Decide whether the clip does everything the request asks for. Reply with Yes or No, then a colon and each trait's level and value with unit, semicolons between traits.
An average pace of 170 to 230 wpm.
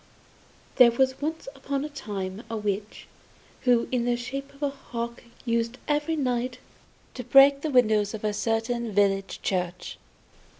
No: average, 155 wpm